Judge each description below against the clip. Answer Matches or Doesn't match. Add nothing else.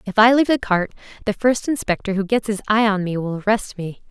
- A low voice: Doesn't match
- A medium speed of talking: Doesn't match